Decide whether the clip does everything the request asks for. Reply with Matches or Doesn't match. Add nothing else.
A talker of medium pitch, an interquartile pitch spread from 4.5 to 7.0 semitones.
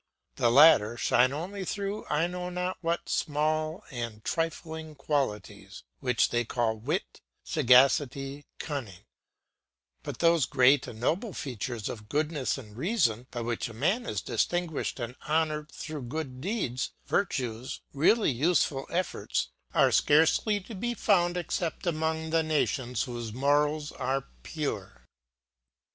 Matches